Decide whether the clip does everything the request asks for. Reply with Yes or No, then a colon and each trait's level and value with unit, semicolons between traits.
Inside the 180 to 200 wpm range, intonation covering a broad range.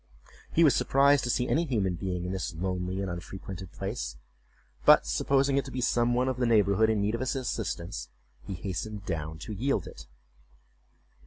Yes: average, 185 wpm; wide, 5.7 semitones